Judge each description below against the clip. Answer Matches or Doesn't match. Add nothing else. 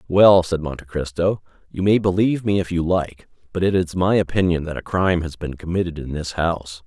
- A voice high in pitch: Doesn't match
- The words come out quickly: Matches